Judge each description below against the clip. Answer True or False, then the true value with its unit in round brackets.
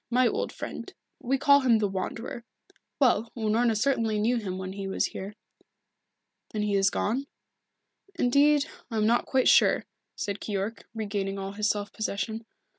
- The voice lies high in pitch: True (220 Hz)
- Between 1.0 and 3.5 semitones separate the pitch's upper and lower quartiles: True (3.1 semitones)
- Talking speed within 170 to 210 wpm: False (160 wpm)